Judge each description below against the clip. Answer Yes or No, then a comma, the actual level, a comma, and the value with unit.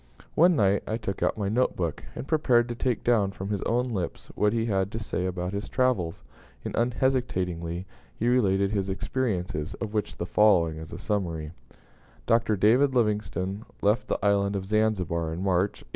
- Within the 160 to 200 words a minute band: Yes, average, 185 wpm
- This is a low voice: Yes, low, 100 Hz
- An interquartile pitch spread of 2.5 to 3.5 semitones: No, average, 4.0 semitones